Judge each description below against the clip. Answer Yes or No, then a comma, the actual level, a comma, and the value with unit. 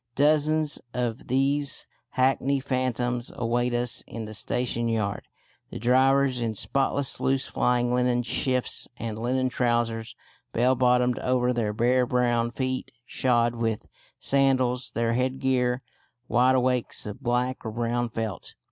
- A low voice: Yes, low, 125 Hz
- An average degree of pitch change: No, narrow, 1.7 semitones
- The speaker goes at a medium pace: No, slow, 130 wpm